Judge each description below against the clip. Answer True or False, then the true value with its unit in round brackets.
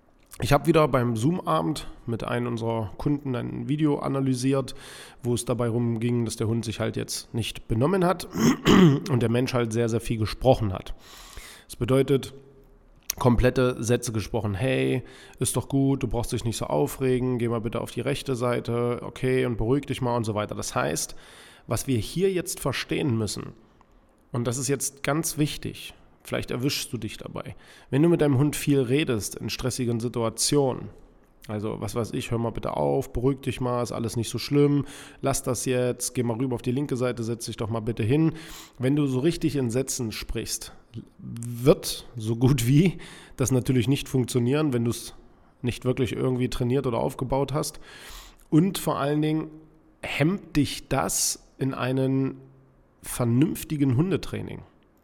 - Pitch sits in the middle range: False (125 Hz)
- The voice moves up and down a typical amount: True (3.0 semitones)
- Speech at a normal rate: True (175 wpm)